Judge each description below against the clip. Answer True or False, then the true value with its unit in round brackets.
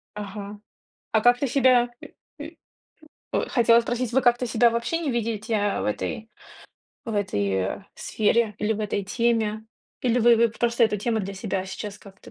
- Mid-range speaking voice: False (225 Hz)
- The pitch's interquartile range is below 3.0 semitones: True (2.5 semitones)